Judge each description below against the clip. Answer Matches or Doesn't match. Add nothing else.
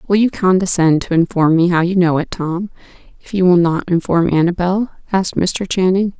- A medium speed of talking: Matches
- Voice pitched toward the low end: Doesn't match